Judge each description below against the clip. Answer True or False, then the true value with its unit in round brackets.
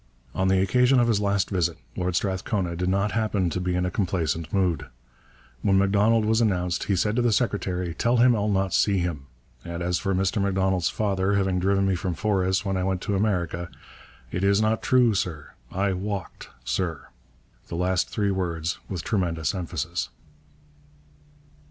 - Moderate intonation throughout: False (2.3 semitones)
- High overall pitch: False (95 Hz)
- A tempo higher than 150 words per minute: True (175 wpm)